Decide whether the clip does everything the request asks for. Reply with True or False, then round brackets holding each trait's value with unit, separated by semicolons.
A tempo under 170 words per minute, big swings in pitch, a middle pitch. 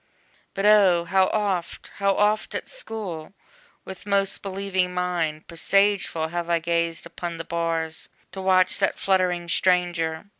False (140 wpm; 2.7 semitones; 180 Hz)